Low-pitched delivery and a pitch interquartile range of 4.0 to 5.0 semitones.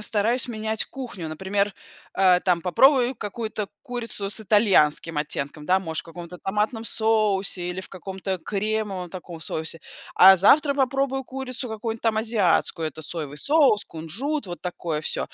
No: high, 200 Hz; average, 4.7 semitones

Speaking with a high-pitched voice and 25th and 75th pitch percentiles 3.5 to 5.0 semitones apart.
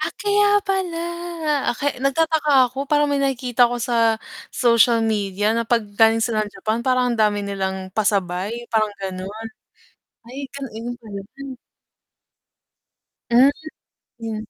Yes: high, 235 Hz; average, 4.3 semitones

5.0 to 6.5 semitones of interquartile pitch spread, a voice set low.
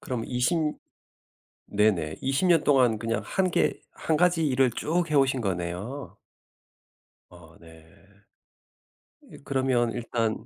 Yes: wide, 5.4 semitones; low, 125 Hz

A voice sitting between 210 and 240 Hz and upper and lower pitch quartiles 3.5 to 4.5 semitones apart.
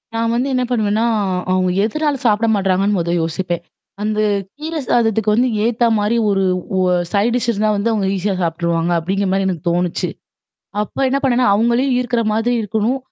Yes: high, 215 Hz; average, 3.9 semitones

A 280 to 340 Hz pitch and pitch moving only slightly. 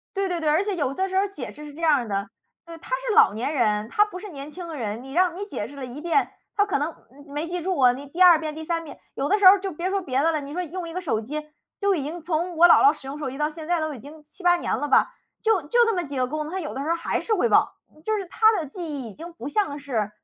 No: very high, 320 Hz; average, 4.5 semitones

